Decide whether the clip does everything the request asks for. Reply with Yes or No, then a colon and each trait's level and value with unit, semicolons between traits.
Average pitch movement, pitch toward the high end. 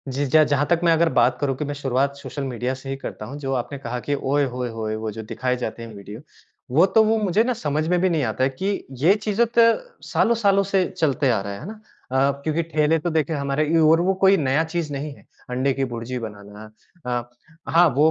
No: average, 4.7 semitones; medium, 140 Hz